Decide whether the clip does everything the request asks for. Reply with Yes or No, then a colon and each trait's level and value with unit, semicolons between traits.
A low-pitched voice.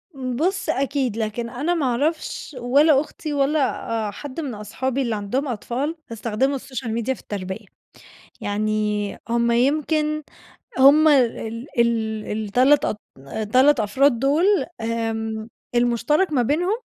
No: very high, 250 Hz